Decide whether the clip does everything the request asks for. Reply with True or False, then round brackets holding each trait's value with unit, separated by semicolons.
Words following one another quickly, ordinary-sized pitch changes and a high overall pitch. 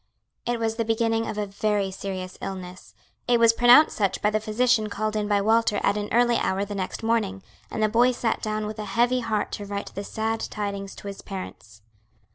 False (215 wpm; 2.2 semitones; 215 Hz)